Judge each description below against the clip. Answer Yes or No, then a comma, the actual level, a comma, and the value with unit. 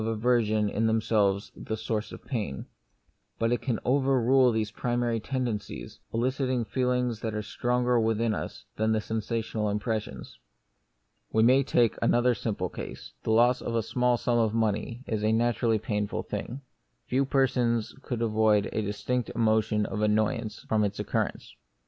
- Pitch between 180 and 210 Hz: No, low, 115 Hz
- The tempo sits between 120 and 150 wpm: No, average, 160 wpm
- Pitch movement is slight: Yes, narrow, 2.3 semitones